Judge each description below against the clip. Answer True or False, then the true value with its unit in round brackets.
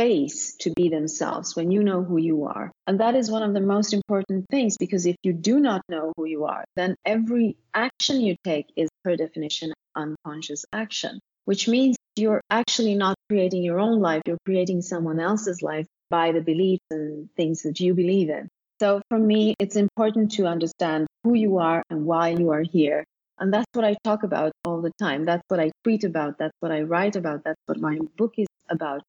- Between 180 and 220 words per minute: True (205 wpm)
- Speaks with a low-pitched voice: False (185 Hz)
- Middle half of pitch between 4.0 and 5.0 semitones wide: True (4.6 semitones)